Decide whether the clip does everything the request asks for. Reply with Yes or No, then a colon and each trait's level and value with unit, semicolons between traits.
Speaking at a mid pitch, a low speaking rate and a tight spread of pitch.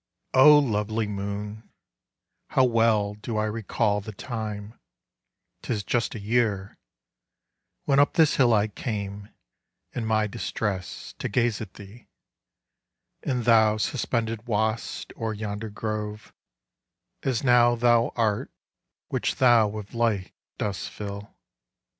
No: low, 110 Hz; slow, 115 wpm; narrow, 2.3 semitones